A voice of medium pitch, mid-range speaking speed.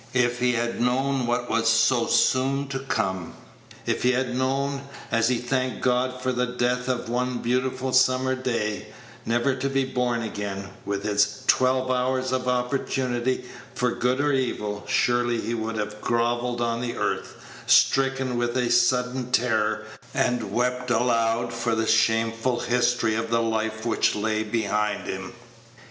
No: low, 120 Hz; average, 155 wpm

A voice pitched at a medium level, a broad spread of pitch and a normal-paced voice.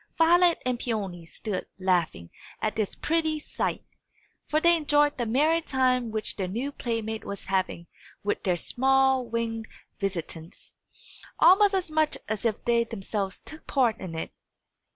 No: high, 230 Hz; wide, 6.8 semitones; average, 150 wpm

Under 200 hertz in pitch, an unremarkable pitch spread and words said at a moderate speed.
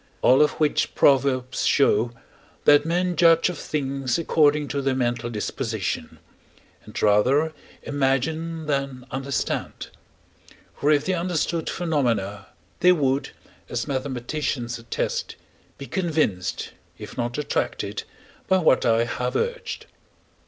No: medium, 140 Hz; average, 4.3 semitones; slow, 115 wpm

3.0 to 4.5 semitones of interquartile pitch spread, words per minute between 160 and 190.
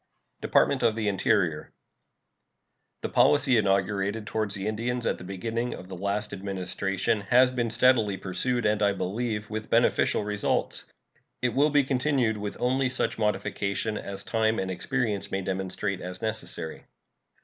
No: average, 3.4 semitones; average, 150 wpm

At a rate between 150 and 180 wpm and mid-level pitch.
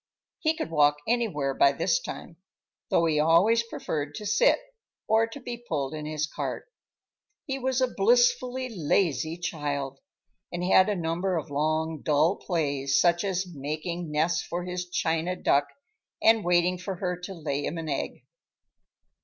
Yes: average, 155 wpm; medium, 170 Hz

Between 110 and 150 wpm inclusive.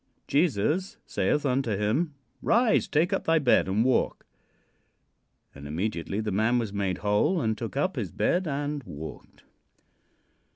Yes: average, 140 wpm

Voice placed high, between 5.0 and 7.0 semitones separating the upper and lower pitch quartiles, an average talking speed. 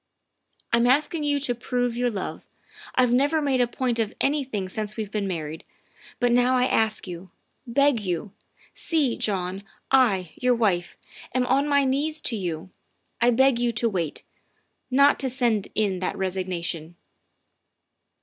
Yes: high, 235 Hz; average, 5.3 semitones; average, 160 wpm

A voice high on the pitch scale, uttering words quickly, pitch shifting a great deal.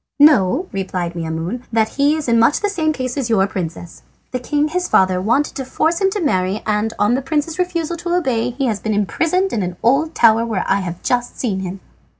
Yes: high, 240 Hz; fast, 220 wpm; wide, 8.0 semitones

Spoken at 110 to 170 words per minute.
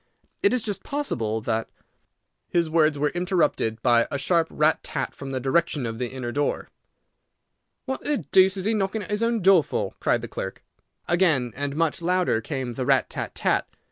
No: average, 190 wpm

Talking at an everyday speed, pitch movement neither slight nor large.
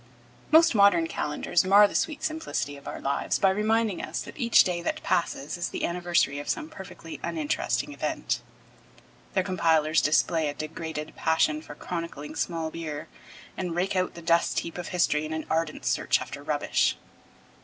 Yes: average, 170 wpm; average, 3.8 semitones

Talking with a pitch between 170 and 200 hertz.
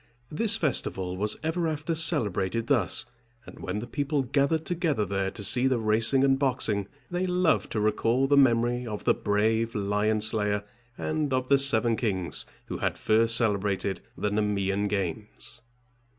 No: low, 115 Hz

